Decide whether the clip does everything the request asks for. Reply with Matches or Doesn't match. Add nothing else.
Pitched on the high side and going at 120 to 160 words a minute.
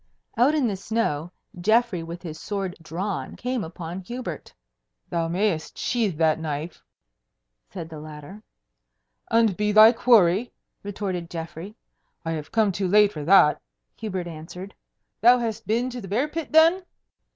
Matches